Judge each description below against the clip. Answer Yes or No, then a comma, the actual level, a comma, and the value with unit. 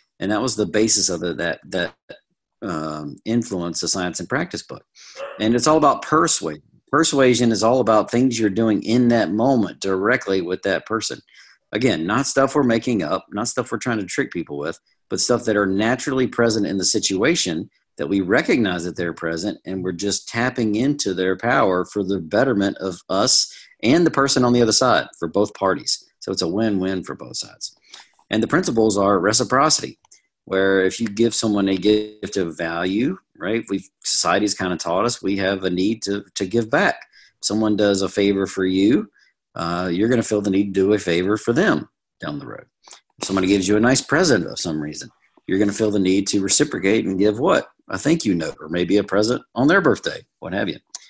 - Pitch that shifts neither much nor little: Yes, average, 3.3 semitones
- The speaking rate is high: Yes, fast, 210 wpm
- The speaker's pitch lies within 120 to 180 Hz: No, low, 105 Hz